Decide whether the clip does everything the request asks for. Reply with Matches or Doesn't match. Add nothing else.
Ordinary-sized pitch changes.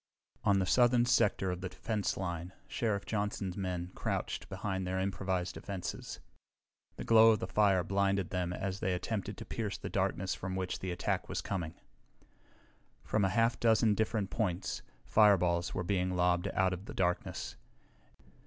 Doesn't match